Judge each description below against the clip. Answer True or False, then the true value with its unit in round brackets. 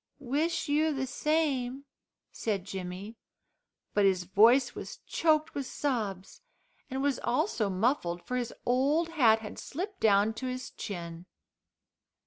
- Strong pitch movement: True (6.2 semitones)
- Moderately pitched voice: False (245 Hz)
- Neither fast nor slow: False (130 wpm)